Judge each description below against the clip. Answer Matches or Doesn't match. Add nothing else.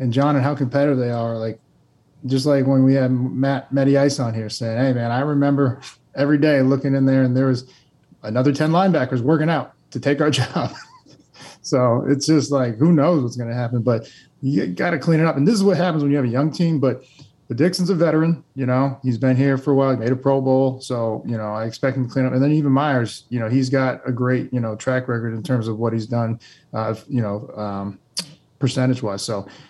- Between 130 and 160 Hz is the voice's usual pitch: Matches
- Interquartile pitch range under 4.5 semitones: Matches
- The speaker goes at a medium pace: Doesn't match